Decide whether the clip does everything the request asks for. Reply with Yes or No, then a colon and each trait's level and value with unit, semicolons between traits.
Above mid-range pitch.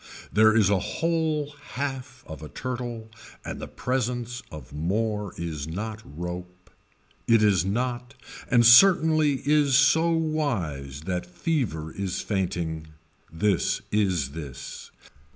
No: low, 110 Hz